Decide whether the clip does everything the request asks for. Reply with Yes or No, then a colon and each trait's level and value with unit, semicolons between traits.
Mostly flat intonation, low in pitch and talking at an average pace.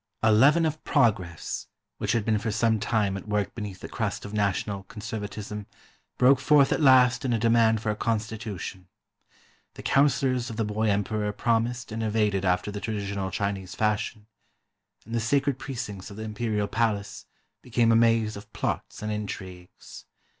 Yes: narrow, 2.2 semitones; low, 110 Hz; average, 170 wpm